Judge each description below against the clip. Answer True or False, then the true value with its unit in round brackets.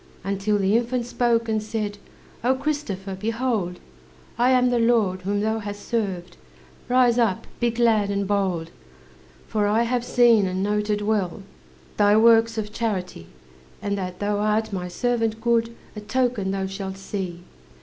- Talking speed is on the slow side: False (155 wpm)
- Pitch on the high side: True (210 Hz)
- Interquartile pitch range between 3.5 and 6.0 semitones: False (3.0 semitones)